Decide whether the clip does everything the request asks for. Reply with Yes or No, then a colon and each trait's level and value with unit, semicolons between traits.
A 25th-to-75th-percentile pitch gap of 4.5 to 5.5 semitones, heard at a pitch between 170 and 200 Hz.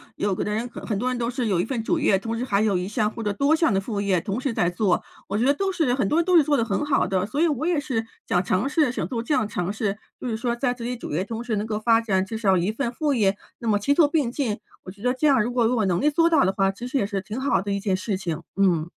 No: average, 5.0 semitones; high, 225 Hz